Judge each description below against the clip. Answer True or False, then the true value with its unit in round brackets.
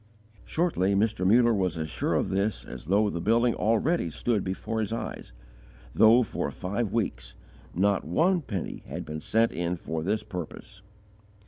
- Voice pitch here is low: True (100 Hz)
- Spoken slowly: False (160 wpm)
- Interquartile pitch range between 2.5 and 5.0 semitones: True (4.2 semitones)